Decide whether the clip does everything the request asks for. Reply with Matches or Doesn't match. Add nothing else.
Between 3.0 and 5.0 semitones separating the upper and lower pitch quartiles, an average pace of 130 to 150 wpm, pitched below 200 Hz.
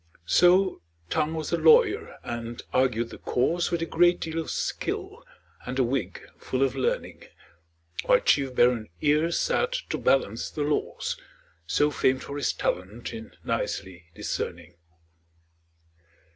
Doesn't match